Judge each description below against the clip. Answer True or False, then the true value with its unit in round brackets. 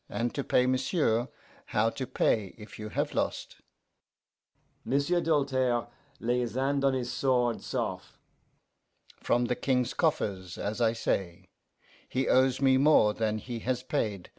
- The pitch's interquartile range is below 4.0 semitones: True (3.1 semitones)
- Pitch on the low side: True (125 Hz)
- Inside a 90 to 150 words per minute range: True (145 wpm)